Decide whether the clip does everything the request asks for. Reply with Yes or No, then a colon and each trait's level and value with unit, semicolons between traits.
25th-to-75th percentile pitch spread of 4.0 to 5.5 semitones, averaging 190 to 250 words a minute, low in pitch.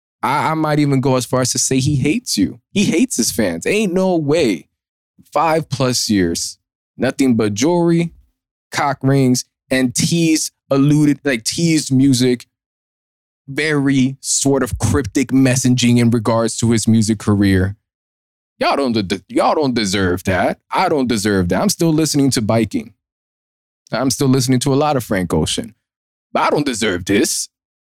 No: average, 5.0 semitones; average, 160 wpm; low, 130 Hz